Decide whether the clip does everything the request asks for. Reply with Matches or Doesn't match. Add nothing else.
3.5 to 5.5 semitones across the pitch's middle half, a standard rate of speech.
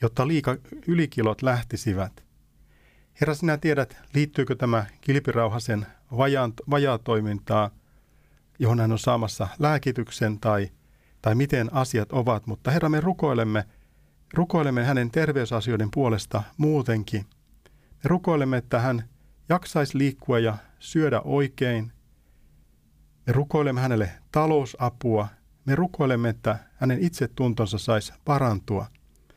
Matches